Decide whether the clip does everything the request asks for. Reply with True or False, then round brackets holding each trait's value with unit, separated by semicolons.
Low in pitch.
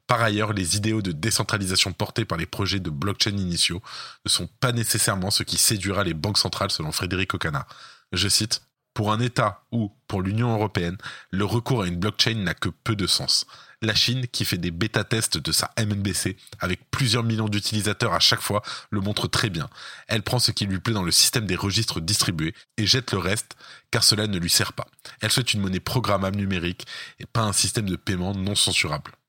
True (105 Hz)